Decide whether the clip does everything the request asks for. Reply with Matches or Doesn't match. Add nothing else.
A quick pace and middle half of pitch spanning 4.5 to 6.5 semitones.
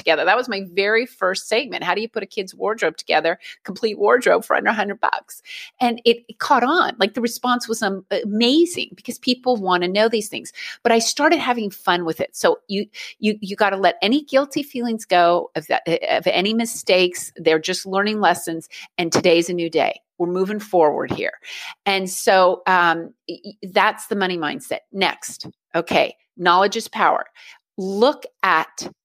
Doesn't match